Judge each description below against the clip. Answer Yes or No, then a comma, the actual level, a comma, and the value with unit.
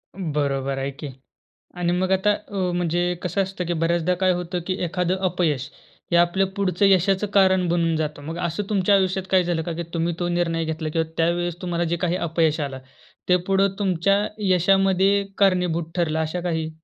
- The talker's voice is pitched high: No, medium, 175 Hz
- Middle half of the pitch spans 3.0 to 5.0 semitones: No, narrow, 2.4 semitones